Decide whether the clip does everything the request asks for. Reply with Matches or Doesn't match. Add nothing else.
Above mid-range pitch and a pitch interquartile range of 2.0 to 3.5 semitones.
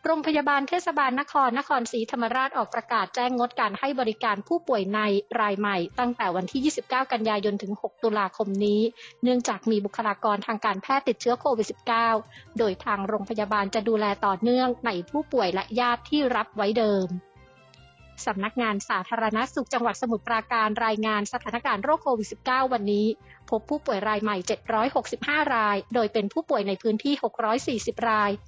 Matches